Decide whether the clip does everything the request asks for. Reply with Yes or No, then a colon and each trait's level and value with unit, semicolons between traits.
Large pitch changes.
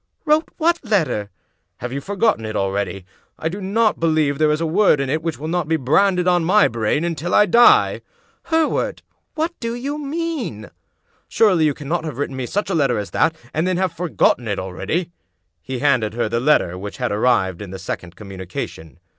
Yes: wide, 9.0 semitones